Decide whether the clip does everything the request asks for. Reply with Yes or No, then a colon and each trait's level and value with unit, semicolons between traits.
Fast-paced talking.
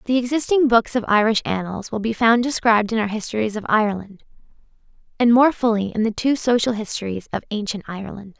No: average, 185 wpm